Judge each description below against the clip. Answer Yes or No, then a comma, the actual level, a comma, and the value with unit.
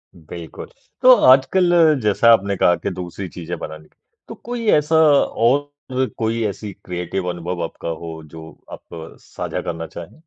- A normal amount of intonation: No, wide, 7.8 semitones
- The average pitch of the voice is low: Yes, low, 100 Hz